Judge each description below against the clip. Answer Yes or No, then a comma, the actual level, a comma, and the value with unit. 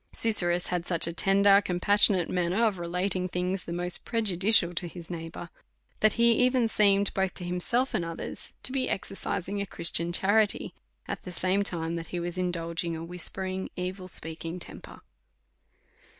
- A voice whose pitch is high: No, medium, 180 Hz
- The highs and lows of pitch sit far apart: No, narrow, 2.6 semitones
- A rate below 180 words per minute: Yes, average, 165 wpm